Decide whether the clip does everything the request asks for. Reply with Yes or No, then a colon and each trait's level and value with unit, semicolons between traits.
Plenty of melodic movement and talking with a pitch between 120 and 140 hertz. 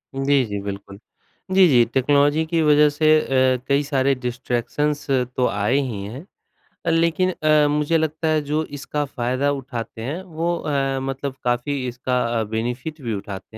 No: average, 3.5 semitones; low, 135 Hz